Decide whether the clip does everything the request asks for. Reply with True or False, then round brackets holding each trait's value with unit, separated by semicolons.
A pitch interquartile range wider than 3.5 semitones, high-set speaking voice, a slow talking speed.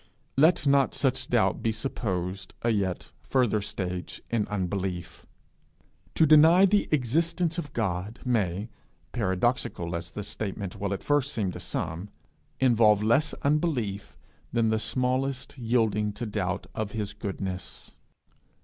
False (5.3 semitones; 110 Hz; 130 wpm)